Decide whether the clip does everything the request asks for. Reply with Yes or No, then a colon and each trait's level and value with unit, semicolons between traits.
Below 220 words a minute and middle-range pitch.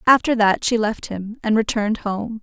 No: average, 200 wpm; high, 220 Hz